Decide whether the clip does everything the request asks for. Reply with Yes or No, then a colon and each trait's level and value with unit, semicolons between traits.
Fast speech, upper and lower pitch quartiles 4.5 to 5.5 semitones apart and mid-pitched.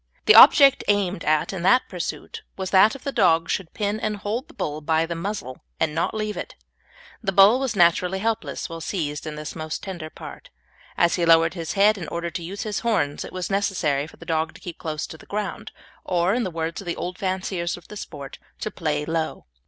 No: fast, 225 wpm; average, 4.0 semitones; medium, 175 Hz